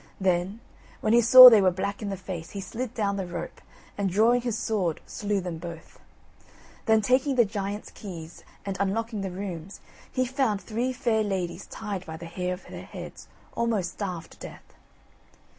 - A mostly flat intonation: No, average, 3.6 semitones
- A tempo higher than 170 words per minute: Yes, average, 180 wpm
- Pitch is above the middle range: Yes, high, 200 Hz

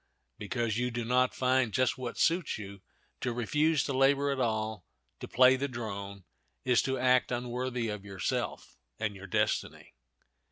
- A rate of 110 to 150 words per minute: No, average, 160 wpm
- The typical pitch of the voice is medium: No, low, 125 Hz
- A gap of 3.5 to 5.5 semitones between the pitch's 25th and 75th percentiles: No, average, 3.0 semitones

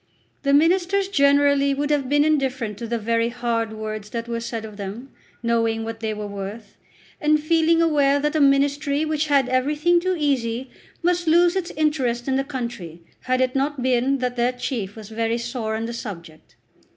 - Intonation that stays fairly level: No, average, 4.4 semitones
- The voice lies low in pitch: No, very high, 255 Hz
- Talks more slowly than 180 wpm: No, average, 190 wpm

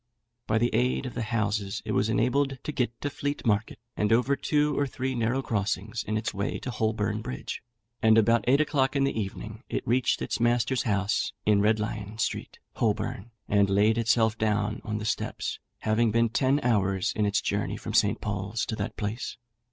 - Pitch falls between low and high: No, low, 110 Hz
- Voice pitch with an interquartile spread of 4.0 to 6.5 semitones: No, average, 2.8 semitones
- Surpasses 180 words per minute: Yes, average, 195 wpm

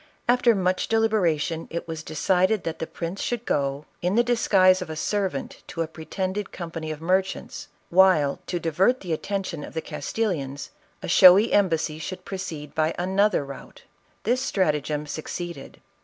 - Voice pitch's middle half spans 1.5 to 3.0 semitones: No, average, 3.8 semitones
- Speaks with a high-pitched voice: No, medium, 180 Hz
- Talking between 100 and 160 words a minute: Yes, average, 155 wpm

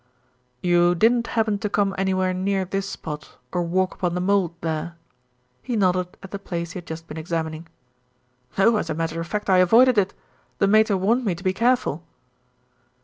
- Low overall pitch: No, medium, 185 Hz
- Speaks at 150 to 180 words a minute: No, average, 190 wpm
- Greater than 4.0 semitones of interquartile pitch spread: No, average, 3.1 semitones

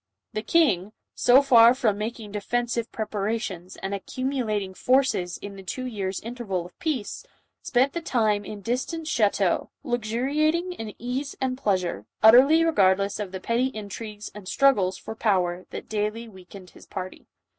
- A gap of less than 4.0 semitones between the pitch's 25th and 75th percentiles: No, average, 4.4 semitones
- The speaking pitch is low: No, high, 220 Hz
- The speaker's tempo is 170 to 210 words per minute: No, average, 155 wpm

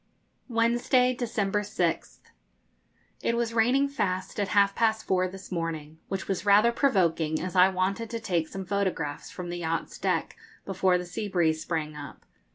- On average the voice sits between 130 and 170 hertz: No, high, 190 Hz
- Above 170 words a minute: No, average, 165 wpm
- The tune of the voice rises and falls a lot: No, average, 4.4 semitones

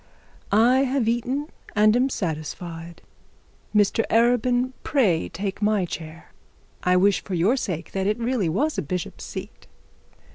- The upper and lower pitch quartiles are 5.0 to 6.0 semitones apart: Yes, wide, 5.5 semitones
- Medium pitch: No, high, 210 Hz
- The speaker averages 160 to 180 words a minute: No, slow, 135 wpm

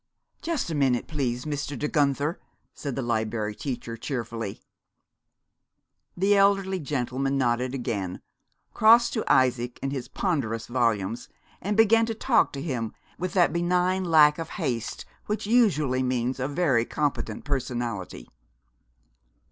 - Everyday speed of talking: No, slow, 130 wpm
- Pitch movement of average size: No, wide, 6.7 semitones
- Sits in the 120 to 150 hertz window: Yes, low, 135 Hz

